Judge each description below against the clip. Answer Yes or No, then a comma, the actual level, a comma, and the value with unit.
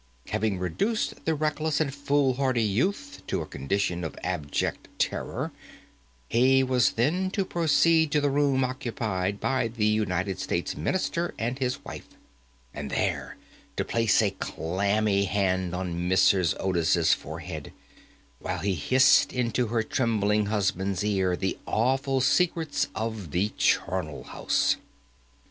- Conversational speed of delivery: No, slow, 130 wpm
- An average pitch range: No, wide, 6.2 semitones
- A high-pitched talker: No, low, 110 Hz